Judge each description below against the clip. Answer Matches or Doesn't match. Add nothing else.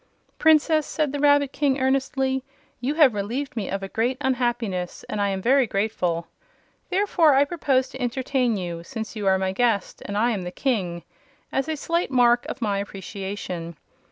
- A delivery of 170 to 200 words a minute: Matches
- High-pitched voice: Matches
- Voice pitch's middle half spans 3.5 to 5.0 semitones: Doesn't match